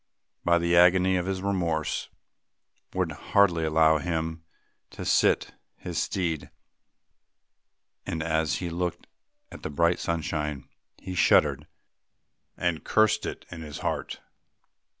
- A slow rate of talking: Yes, slow, 120 wpm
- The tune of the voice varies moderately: No, narrow, 2.1 semitones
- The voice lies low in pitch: Yes, very low, 85 Hz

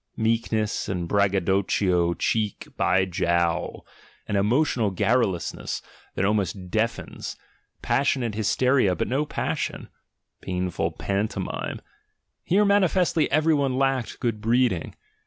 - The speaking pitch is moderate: No, low, 105 Hz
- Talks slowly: Yes, slow, 100 wpm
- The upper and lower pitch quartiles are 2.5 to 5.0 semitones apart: No, wide, 5.4 semitones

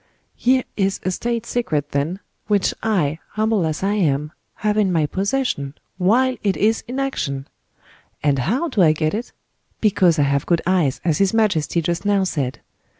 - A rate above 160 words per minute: Yes, average, 175 wpm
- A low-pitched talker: No, medium, 185 Hz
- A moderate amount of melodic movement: No, wide, 6.0 semitones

